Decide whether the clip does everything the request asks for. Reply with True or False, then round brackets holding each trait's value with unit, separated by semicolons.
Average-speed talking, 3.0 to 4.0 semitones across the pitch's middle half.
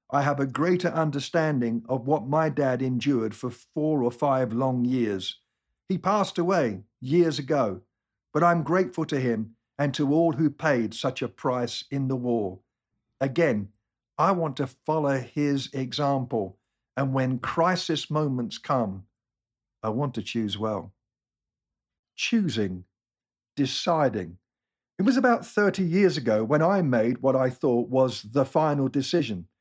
False (145 wpm; 5.0 semitones)